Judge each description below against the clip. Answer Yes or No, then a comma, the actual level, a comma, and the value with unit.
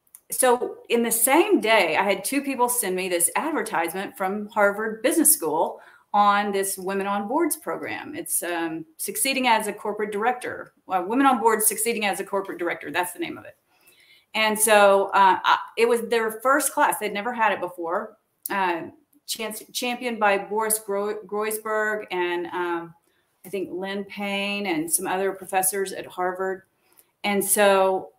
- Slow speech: No, average, 170 wpm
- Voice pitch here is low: No, high, 210 Hz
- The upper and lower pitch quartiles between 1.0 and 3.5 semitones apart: No, average, 4.2 semitones